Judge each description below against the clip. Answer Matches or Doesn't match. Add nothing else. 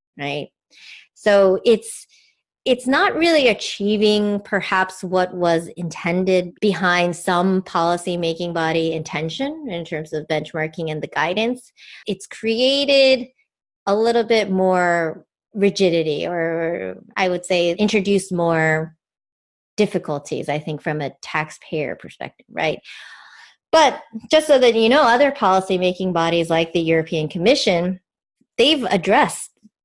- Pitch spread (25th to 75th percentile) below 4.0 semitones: Doesn't match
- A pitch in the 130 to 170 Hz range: Doesn't match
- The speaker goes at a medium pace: Doesn't match